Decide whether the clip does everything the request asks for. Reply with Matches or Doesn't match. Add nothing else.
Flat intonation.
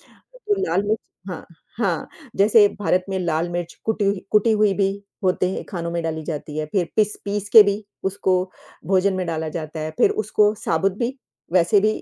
Doesn't match